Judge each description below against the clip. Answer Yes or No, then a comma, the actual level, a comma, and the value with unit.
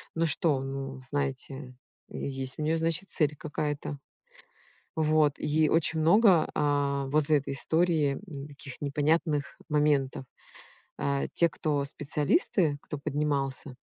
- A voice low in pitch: No, medium, 145 Hz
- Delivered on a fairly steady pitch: Yes, narrow, 2.1 semitones